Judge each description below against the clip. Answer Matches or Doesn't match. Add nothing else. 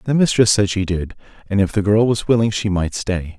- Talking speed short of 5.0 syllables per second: Doesn't match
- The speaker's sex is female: Doesn't match